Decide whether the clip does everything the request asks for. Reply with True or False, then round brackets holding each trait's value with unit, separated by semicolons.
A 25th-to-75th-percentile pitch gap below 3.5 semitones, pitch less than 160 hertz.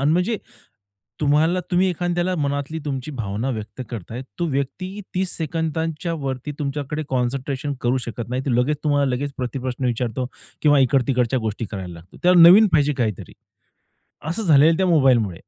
False (4.6 semitones; 140 Hz)